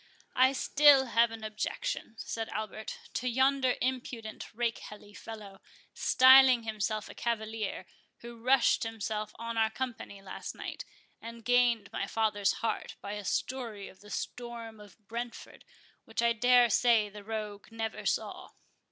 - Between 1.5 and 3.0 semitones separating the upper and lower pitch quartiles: Yes, narrow, 2.4 semitones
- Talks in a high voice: Yes, high, 225 Hz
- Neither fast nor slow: Yes, average, 145 wpm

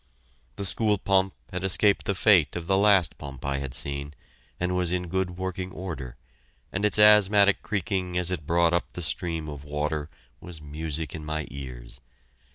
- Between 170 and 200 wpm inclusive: Yes, average, 175 wpm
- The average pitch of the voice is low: Yes, very low, 90 Hz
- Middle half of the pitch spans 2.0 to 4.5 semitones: Yes, average, 4.1 semitones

